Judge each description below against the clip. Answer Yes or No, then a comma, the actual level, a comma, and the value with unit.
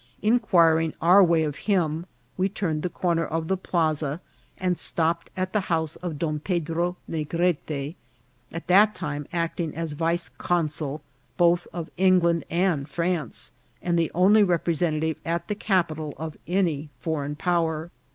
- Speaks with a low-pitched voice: No, medium, 170 Hz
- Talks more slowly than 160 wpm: Yes, average, 145 wpm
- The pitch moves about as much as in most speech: No, narrow, 2.3 semitones